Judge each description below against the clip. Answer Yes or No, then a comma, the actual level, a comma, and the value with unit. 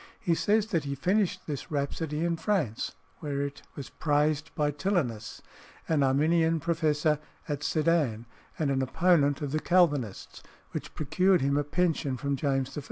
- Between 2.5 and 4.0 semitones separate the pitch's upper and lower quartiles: Yes, average, 3.1 semitones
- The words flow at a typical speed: Yes, average, 160 wpm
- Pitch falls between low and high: Yes, medium, 150 Hz